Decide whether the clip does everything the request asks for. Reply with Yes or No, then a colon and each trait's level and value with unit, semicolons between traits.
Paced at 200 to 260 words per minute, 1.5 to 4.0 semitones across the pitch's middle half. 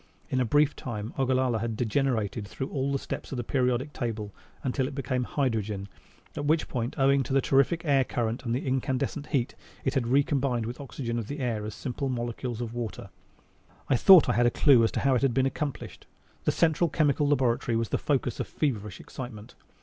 Yes: fast, 205 wpm; average, 2.9 semitones